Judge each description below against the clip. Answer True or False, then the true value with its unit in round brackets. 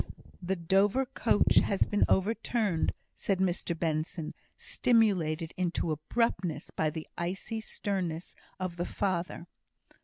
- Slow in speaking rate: True (115 wpm)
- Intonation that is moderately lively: True (3.7 semitones)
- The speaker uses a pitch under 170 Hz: False (185 Hz)